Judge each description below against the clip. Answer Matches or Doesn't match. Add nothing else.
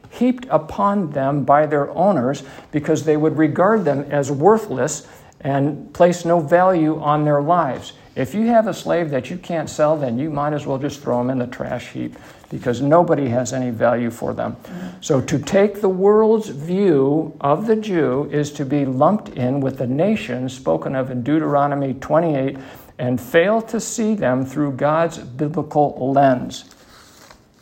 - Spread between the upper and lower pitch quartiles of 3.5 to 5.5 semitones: Matches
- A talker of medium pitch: Matches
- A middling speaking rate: Matches